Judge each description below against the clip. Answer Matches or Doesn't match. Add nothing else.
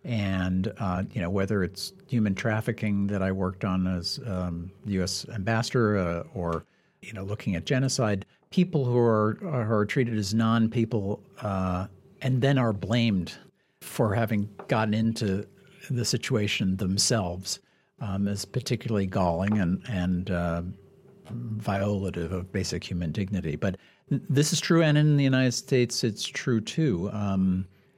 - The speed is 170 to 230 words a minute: Doesn't match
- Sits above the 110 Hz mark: Doesn't match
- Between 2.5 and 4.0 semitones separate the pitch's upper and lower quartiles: Doesn't match